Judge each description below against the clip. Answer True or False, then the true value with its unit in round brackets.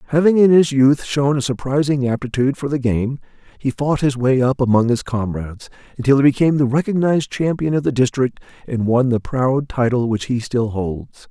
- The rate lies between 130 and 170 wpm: False (195 wpm)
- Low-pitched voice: True (130 Hz)